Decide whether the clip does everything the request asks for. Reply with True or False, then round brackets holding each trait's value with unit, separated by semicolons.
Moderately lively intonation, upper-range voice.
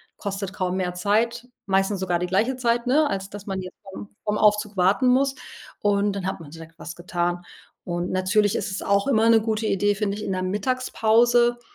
True (3.2 semitones; 200 Hz)